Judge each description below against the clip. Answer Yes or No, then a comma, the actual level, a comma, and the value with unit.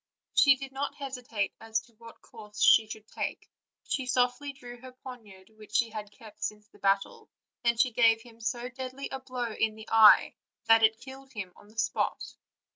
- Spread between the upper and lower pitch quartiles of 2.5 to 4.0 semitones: Yes, average, 2.8 semitones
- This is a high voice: Yes, high, 230 Hz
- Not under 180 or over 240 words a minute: Yes, average, 190 wpm